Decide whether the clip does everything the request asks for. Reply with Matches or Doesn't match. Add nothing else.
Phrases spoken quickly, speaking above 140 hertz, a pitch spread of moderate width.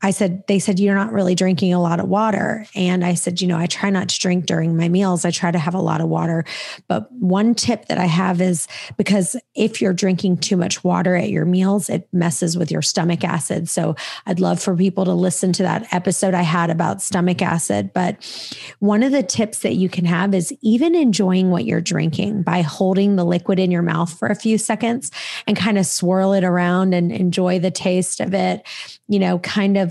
Doesn't match